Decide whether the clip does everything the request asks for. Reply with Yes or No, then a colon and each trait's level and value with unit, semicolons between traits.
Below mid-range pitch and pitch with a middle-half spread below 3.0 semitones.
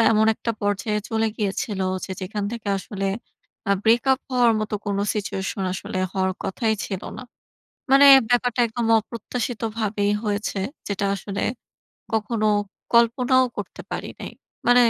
No: high, 215 Hz; narrow, 2.6 semitones